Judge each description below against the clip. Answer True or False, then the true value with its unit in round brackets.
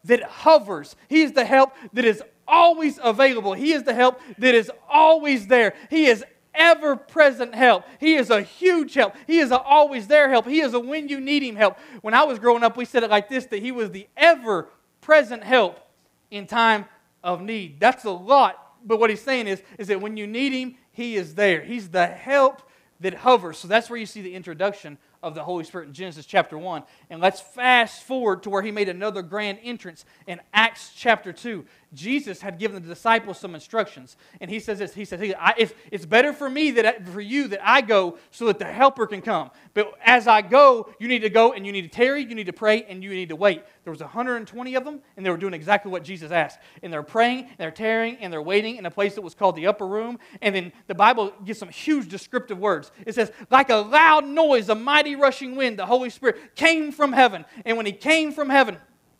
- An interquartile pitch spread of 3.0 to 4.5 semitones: False (4.9 semitones)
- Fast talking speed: True (230 wpm)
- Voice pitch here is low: False (225 Hz)